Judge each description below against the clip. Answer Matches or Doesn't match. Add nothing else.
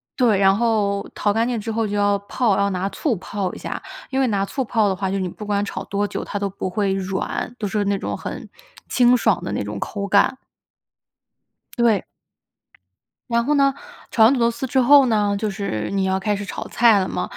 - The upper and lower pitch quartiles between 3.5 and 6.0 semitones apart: Doesn't match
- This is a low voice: Doesn't match